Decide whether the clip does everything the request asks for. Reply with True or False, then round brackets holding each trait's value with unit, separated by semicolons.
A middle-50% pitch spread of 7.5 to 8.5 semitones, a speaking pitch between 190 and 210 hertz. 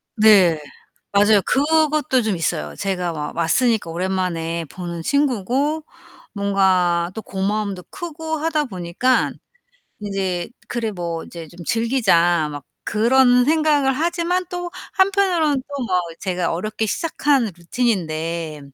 True (8.2 semitones; 205 Hz)